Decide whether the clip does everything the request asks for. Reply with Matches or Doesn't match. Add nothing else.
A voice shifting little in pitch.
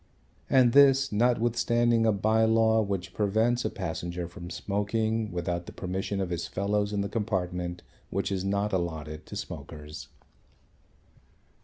Doesn't match